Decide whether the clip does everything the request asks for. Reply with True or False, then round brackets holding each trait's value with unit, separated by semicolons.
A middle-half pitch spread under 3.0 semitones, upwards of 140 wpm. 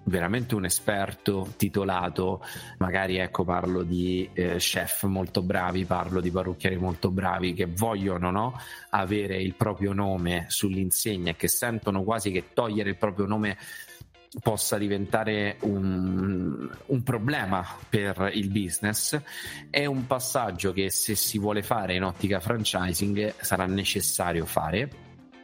False (2.5 semitones; 130 wpm)